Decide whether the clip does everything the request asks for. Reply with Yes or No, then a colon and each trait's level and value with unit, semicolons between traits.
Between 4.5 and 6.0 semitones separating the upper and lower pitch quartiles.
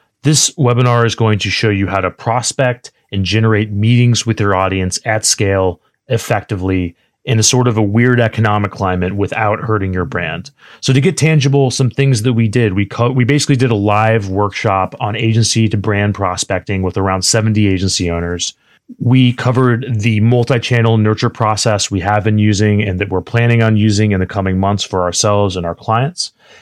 No: average, 3.4 semitones